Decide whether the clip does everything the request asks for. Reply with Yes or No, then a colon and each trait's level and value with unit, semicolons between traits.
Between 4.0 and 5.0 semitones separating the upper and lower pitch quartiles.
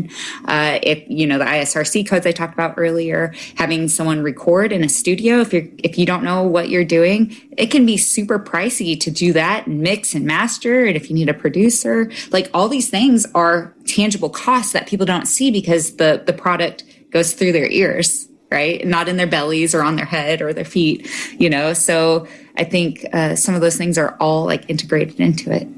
Yes: average, 4.4 semitones